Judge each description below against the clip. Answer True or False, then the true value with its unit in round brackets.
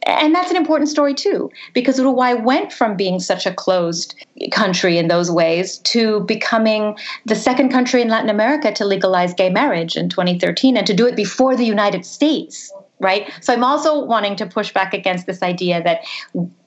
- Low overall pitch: False (215 Hz)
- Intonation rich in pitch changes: True (5.8 semitones)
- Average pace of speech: True (185 wpm)